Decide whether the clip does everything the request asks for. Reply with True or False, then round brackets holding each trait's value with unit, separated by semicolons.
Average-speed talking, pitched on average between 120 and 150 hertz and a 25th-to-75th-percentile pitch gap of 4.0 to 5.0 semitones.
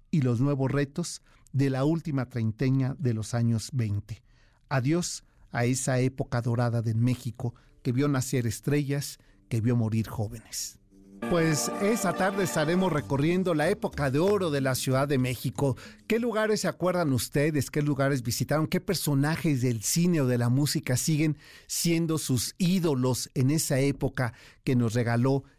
True (155 wpm; 135 Hz; 4.4 semitones)